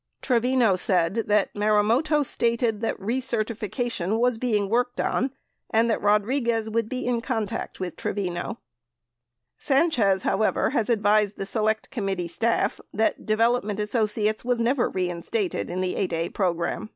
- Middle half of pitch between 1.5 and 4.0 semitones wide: Yes, average, 3.1 semitones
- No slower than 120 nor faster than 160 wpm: Yes, average, 140 wpm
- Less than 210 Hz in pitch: No, high, 220 Hz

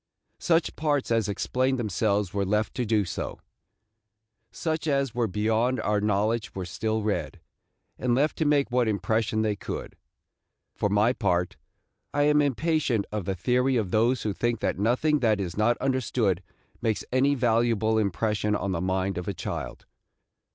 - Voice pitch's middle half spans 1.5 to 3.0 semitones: No, average, 4.0 semitones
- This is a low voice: Yes, low, 110 Hz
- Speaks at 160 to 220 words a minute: Yes, average, 165 wpm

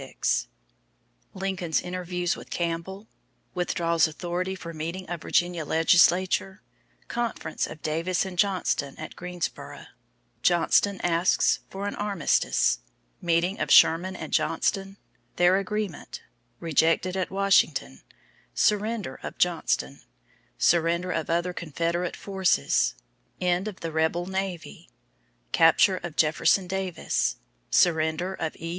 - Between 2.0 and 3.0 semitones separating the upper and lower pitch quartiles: Yes, narrow, 2.6 semitones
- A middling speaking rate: No, slow, 115 wpm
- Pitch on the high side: No, medium, 175 Hz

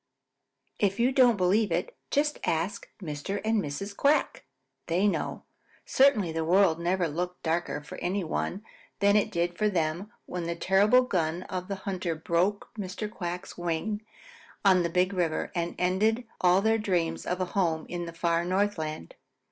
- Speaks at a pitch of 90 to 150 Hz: No, medium, 180 Hz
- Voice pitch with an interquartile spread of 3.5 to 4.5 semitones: No, average, 3.1 semitones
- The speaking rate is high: No, average, 165 wpm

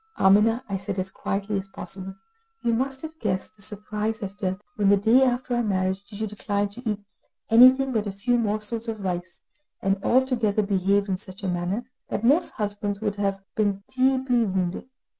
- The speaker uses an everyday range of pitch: Yes, average, 3.0 semitones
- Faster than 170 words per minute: Yes, average, 185 wpm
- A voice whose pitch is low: No, high, 205 Hz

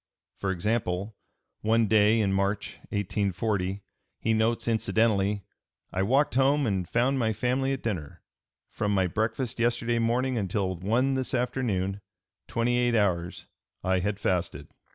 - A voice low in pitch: Yes, low, 110 Hz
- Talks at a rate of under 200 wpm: Yes, slow, 135 wpm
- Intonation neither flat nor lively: Yes, average, 3.5 semitones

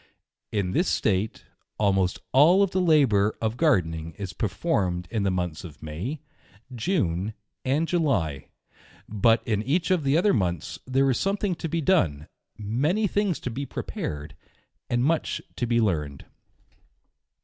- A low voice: Yes, low, 115 Hz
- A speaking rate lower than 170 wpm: Yes, average, 150 wpm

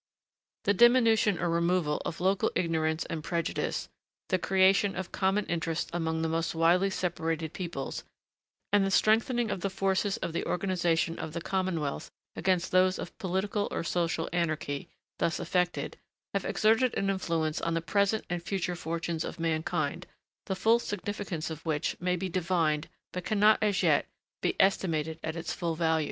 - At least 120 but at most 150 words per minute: No, average, 165 wpm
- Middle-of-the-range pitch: Yes, medium, 175 Hz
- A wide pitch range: No, average, 2.9 semitones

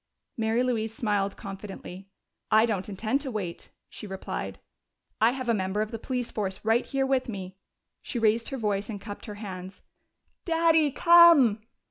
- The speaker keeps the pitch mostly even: No, average, 4.1 semitones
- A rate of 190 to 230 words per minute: No, average, 165 wpm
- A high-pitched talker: Yes, high, 220 Hz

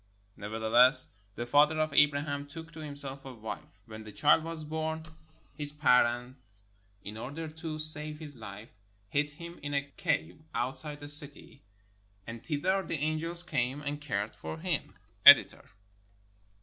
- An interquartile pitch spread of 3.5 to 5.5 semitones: Yes, average, 4.2 semitones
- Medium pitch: Yes, medium, 145 Hz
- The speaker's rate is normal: Yes, average, 150 wpm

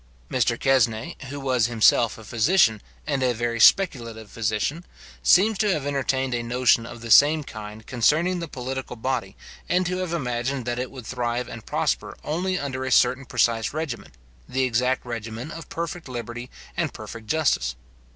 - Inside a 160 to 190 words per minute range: Yes, average, 170 wpm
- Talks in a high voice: No, low, 125 Hz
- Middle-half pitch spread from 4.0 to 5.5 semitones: No, average, 3.6 semitones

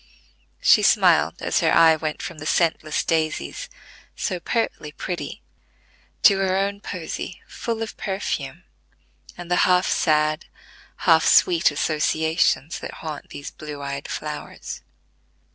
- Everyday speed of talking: No, slow, 125 wpm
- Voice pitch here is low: No, medium, 160 Hz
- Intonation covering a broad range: No, average, 3.7 semitones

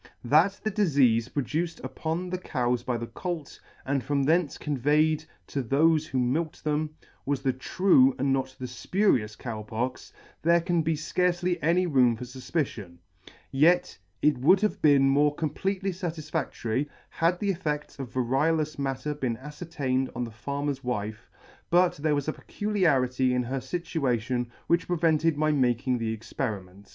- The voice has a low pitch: No, medium, 145 Hz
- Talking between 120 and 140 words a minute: No, average, 160 wpm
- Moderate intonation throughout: Yes, average, 4.5 semitones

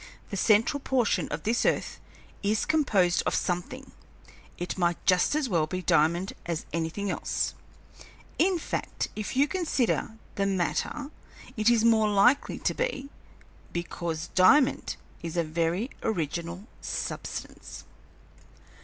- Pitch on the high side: Yes, high, 200 Hz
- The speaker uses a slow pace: Yes, slow, 125 wpm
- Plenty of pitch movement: Yes, wide, 6.6 semitones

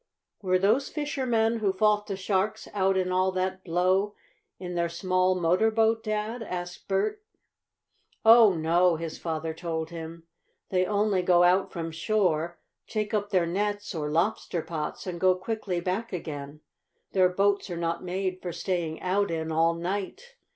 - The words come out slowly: No, average, 160 wpm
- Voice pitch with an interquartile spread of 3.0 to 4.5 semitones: Yes, average, 3.3 semitones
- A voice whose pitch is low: No, medium, 185 Hz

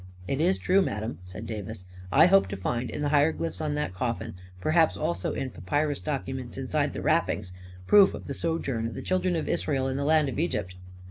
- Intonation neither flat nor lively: No, wide, 7.0 semitones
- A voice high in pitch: No, low, 135 Hz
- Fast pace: Yes, fast, 225 wpm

